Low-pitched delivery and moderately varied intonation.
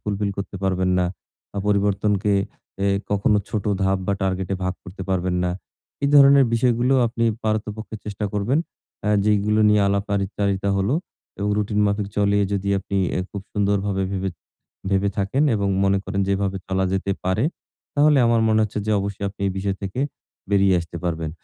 No: low, 100 Hz; narrow, 1.6 semitones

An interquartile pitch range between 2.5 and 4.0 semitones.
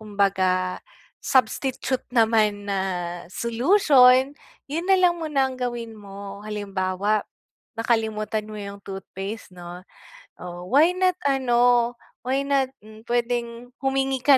No: average, 4.8 semitones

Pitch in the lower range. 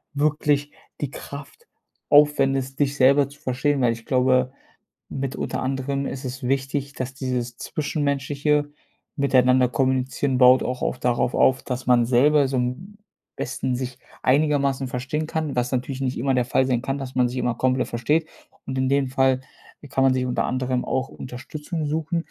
Yes: low, 130 Hz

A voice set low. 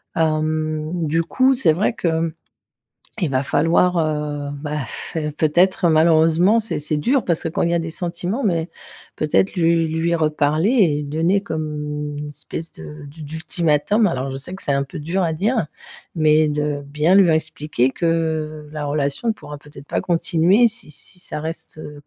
No: medium, 160 Hz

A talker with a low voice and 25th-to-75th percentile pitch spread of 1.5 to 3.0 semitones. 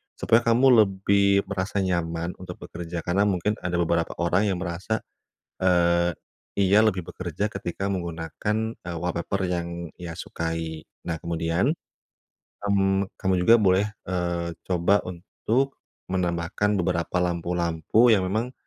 Yes: very low, 90 Hz; average, 2.7 semitones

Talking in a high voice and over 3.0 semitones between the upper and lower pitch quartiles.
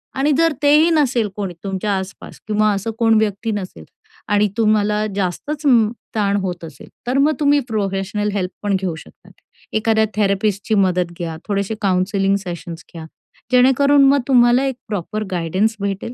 Yes: high, 210 Hz; average, 3.5 semitones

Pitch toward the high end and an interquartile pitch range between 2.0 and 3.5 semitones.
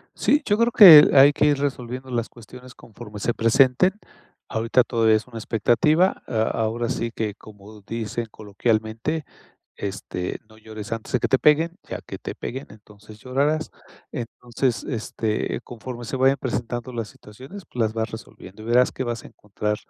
No: low, 120 Hz; average, 3.2 semitones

